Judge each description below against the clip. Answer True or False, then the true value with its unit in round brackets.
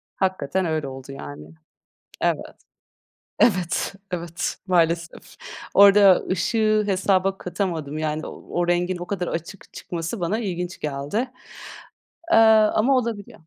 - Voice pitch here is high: False (180 Hz)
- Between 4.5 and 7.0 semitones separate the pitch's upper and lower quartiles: False (3.3 semitones)